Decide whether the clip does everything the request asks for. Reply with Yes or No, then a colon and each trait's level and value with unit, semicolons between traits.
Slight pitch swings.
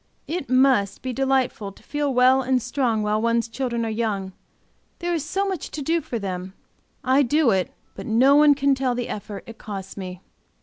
No: average, 4.4 semitones